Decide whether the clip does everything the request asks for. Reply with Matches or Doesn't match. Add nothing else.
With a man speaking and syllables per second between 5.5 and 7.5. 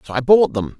Matches